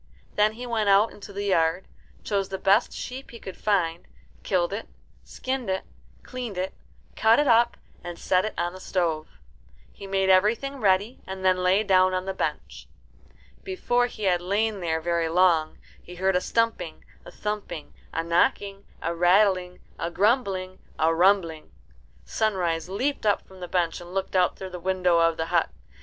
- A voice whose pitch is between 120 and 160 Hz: No, high, 190 Hz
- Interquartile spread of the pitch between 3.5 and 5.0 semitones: No, average, 3.0 semitones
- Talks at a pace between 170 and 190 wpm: Yes, average, 175 wpm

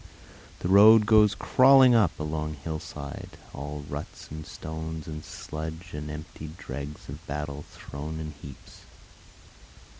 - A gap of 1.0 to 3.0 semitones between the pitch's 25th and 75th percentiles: Yes, average, 2.7 semitones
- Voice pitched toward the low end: Yes, very low, 75 Hz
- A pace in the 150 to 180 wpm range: No, average, 140 wpm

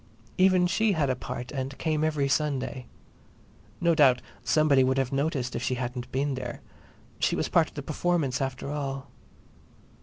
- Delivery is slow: No, average, 170 wpm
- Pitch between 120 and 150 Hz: Yes, low, 135 Hz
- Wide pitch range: No, average, 3.1 semitones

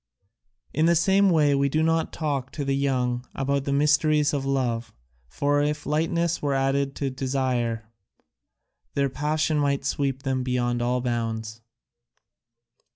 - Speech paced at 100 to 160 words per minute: Yes, average, 145 wpm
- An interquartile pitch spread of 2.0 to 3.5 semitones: Yes, average, 2.9 semitones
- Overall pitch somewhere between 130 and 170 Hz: Yes, medium, 140 Hz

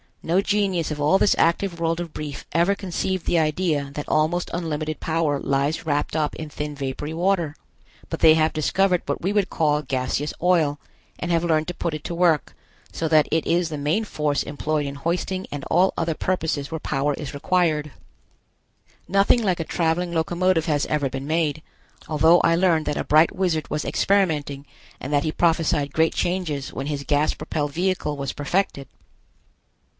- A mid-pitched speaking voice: Yes, medium, 160 Hz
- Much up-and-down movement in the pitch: No, average, 2.9 semitones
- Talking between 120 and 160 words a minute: No, average, 180 wpm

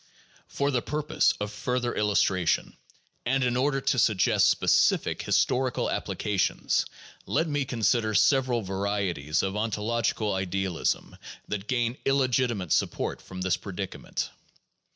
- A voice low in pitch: Yes, low, 110 Hz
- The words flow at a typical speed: No, slow, 120 wpm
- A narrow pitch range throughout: No, average, 4.7 semitones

